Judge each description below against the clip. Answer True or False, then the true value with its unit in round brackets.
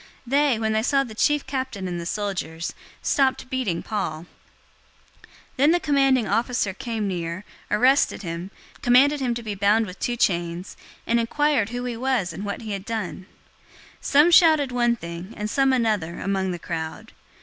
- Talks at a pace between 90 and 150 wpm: False (175 wpm)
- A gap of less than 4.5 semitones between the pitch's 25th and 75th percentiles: False (5.6 semitones)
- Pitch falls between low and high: False (225 Hz)